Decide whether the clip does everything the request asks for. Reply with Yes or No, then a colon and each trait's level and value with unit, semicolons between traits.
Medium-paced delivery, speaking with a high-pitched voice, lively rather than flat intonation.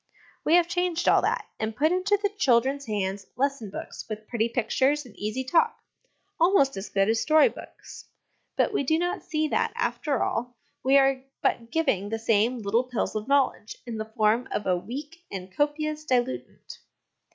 Yes: average, 180 wpm; very high, 255 Hz; wide, 5.9 semitones